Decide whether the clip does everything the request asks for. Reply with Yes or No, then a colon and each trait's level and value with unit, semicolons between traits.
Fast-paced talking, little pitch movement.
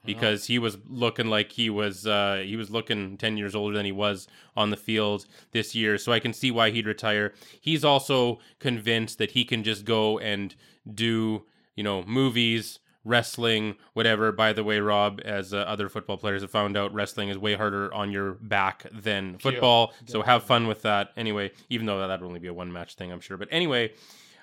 Yes: fast, 210 wpm; narrow, 2.1 semitones